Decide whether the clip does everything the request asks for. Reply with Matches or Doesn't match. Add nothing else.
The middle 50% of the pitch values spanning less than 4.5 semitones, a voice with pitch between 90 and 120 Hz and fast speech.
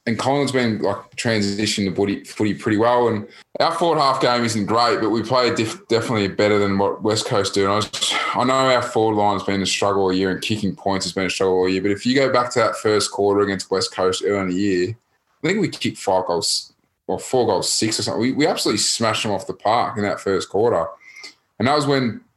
Matches